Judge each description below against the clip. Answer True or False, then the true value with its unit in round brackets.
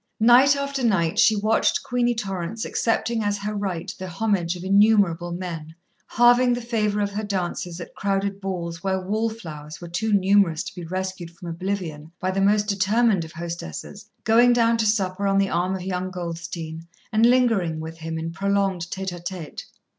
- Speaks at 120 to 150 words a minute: False (185 wpm)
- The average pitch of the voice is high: True (195 Hz)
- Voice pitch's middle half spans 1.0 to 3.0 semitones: False (3.9 semitones)